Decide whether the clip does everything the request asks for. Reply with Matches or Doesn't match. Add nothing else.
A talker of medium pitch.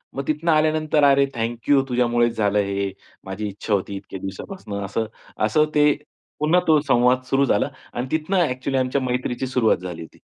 Doesn't match